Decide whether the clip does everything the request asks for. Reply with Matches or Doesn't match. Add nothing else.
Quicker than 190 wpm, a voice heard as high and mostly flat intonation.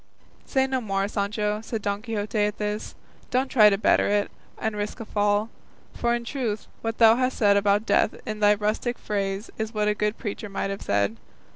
Matches